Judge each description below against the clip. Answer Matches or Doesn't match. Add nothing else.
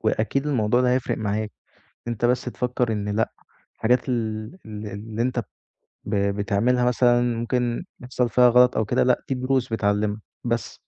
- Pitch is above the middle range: Doesn't match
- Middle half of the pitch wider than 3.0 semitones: Doesn't match